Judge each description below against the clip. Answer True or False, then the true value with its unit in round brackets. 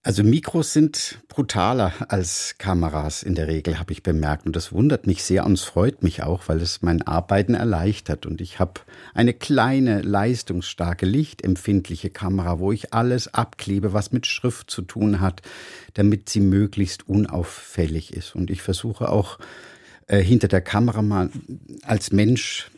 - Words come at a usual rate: True (160 wpm)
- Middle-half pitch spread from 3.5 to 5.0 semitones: True (3.8 semitones)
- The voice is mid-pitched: False (100 Hz)